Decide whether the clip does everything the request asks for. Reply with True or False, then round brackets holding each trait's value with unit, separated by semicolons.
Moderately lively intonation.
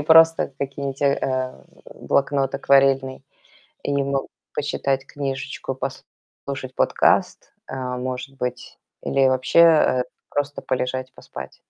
False (1.2 semitones)